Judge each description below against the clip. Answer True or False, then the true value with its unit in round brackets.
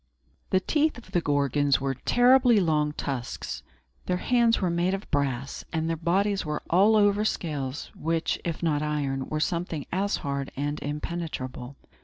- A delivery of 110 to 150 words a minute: False (160 wpm)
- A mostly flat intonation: False (5.1 semitones)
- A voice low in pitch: False (160 Hz)